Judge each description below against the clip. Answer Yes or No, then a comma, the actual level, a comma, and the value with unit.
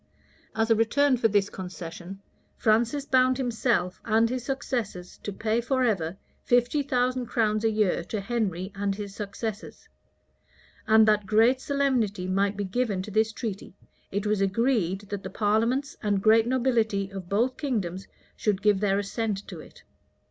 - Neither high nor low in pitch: No, high, 215 Hz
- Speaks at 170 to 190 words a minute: No, average, 155 wpm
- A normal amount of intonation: Yes, average, 3.4 semitones